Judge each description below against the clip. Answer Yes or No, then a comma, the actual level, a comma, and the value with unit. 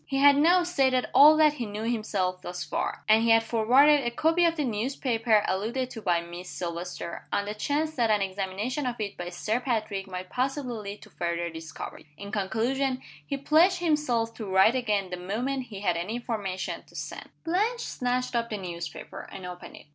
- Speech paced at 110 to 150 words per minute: No, average, 200 wpm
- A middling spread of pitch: No, wide, 5.8 semitones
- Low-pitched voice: No, high, 225 Hz